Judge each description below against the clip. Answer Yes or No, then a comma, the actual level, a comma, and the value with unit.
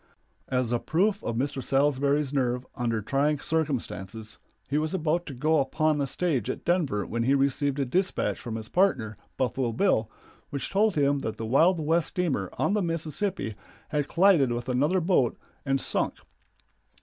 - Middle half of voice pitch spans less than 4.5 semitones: No, average, 4.8 semitones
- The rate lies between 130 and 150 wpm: No, average, 170 wpm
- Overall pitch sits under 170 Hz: Yes, medium, 140 Hz